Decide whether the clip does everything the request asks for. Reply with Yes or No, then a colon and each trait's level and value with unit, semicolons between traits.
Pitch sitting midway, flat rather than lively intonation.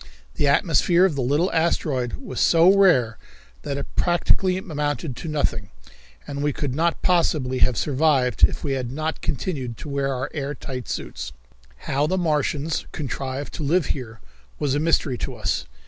No: medium, 145 Hz; average, 3.8 semitones